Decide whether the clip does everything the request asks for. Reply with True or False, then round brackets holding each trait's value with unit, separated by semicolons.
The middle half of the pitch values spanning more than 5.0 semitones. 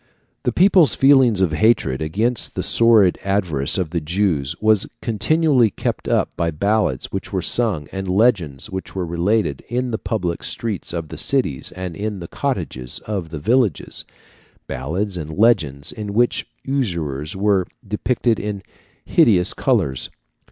True (5.5 semitones)